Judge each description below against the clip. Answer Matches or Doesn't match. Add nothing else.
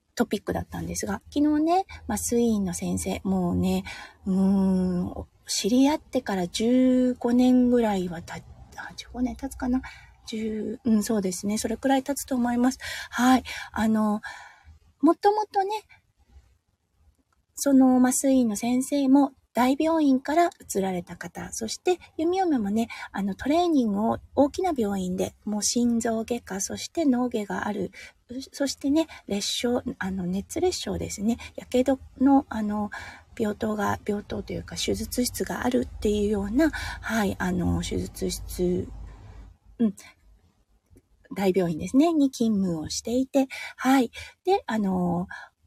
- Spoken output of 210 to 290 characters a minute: Matches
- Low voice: Doesn't match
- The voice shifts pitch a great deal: Matches